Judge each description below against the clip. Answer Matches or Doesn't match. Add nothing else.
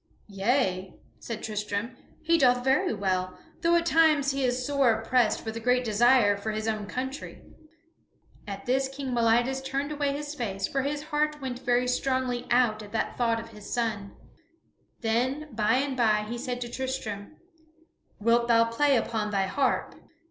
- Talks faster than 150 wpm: Matches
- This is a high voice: Matches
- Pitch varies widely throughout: Doesn't match